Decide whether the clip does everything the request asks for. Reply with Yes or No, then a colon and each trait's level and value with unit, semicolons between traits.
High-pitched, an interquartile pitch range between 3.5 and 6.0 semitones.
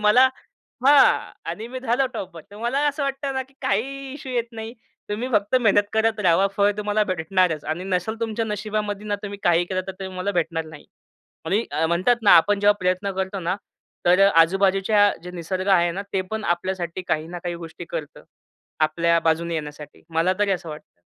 Yes: high, 195 Hz; average, 4.1 semitones